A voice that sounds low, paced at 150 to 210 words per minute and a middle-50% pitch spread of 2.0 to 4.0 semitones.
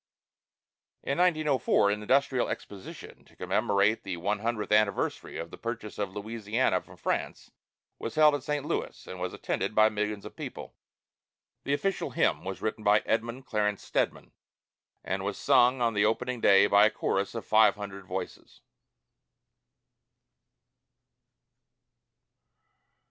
No: low, 110 Hz; average, 140 wpm; average, 3.5 semitones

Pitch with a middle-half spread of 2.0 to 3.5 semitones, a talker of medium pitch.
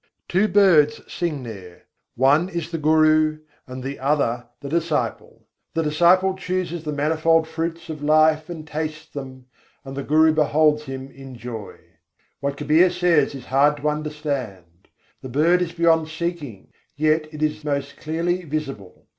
Yes: average, 2.8 semitones; medium, 155 Hz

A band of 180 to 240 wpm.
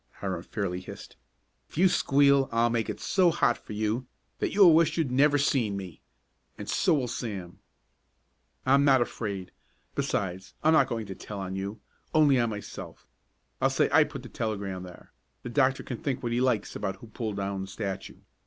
Yes: average, 190 wpm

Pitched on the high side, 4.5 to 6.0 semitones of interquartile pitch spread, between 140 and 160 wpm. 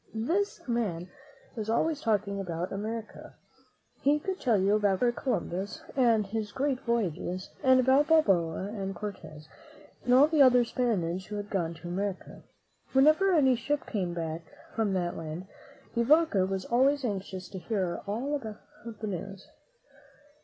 Yes: high, 210 Hz; wide, 5.5 semitones; average, 150 wpm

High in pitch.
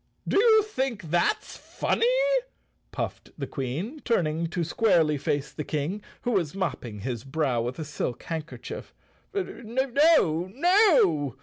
No: medium, 170 Hz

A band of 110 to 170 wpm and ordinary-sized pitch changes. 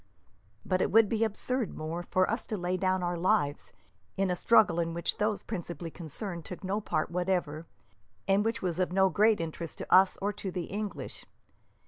No: average, 195 wpm; average, 3.2 semitones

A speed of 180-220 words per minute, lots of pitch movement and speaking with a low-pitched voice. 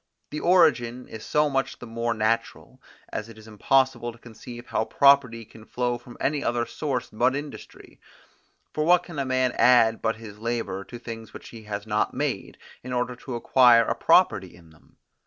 No: average, 190 wpm; average, 2.7 semitones; low, 120 Hz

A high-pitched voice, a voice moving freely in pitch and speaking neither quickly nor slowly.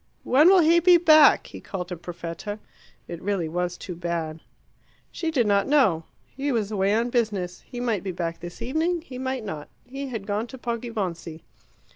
Yes: high, 210 Hz; wide, 6.8 semitones; average, 185 wpm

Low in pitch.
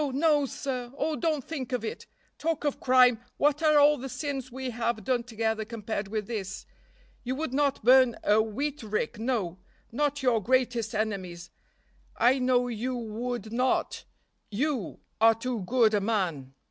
No: high, 245 Hz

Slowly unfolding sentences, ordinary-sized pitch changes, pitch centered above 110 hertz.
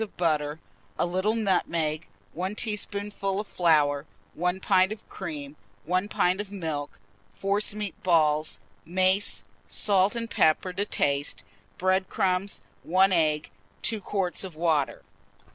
Yes: slow, 125 wpm; average, 4.0 semitones; medium, 185 Hz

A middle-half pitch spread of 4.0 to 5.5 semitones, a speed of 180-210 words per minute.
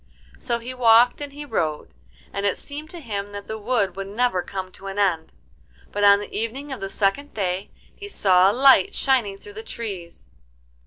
Yes: average, 4.4 semitones; average, 200 wpm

